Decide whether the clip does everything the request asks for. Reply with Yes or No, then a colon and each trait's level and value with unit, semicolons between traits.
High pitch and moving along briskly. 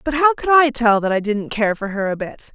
Yes: high, 240 Hz; fast, 305 wpm